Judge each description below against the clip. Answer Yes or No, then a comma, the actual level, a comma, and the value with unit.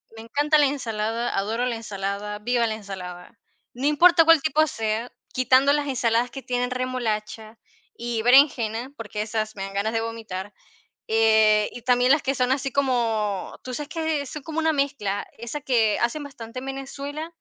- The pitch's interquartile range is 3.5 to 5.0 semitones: Yes, average, 4.1 semitones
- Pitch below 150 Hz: No, high, 240 Hz